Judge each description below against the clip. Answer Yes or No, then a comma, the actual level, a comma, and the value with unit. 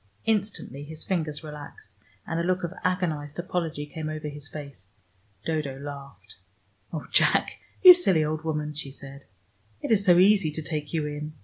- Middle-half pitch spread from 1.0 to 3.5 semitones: Yes, average, 3.0 semitones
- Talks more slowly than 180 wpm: Yes, average, 170 wpm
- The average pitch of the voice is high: No, medium, 155 Hz